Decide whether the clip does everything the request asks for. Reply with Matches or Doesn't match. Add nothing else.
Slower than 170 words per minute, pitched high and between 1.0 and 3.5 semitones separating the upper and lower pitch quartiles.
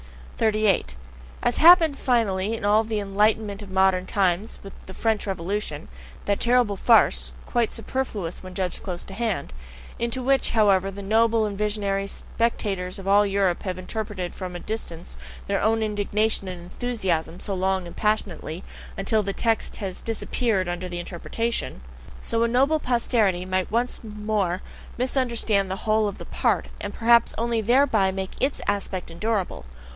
Matches